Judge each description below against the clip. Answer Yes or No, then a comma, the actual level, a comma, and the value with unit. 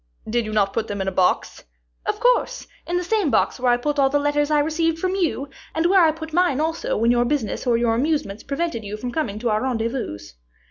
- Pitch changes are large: Yes, wide, 5.9 semitones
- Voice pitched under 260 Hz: No, very high, 275 Hz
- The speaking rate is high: Yes, fast, 240 wpm